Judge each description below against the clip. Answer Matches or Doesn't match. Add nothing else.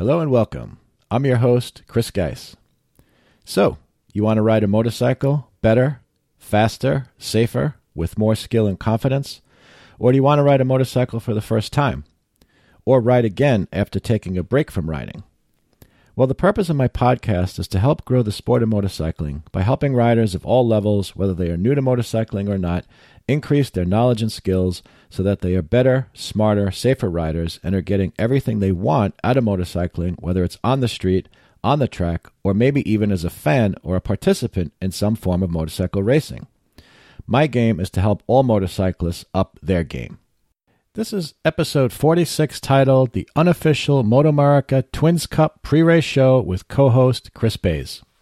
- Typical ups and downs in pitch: Doesn't match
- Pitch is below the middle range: Matches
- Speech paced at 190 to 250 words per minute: Doesn't match